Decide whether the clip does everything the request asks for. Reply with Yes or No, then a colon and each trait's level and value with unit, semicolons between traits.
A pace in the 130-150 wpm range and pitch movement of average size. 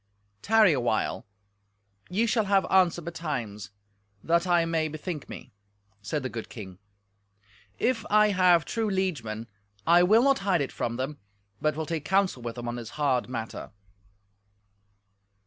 No: average, 145 wpm; wide, 8.4 semitones